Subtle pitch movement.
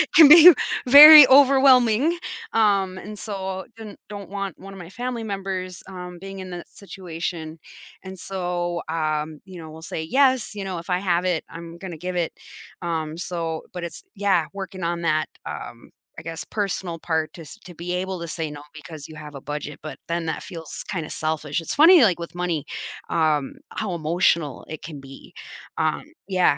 No: average, 3.4 semitones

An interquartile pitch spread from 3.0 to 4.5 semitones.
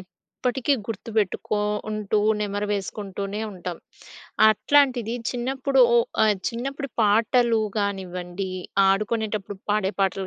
Yes: average, 3.3 semitones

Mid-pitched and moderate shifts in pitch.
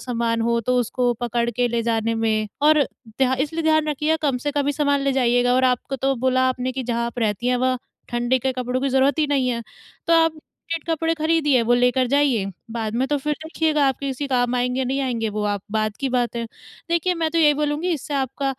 No: very high, 260 Hz; average, 3.4 semitones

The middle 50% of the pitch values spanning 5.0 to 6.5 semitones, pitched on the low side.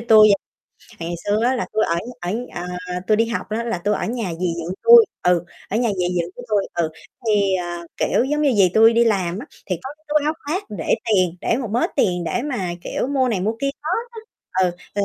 No: average, 5.3 semitones; high, 210 Hz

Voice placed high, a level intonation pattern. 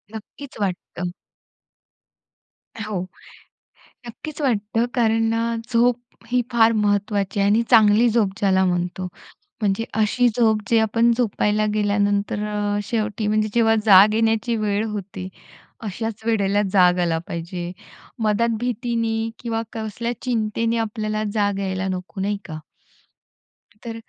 Yes: high, 215 Hz; narrow, 2.2 semitones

